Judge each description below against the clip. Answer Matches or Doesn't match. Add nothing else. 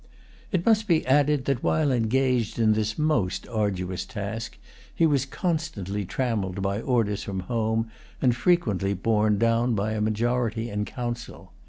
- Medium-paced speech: Matches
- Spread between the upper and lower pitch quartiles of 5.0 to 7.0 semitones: Doesn't match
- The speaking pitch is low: Matches